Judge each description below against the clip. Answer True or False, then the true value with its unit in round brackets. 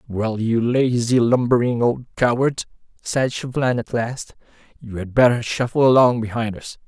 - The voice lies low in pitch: True (120 Hz)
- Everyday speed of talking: True (150 wpm)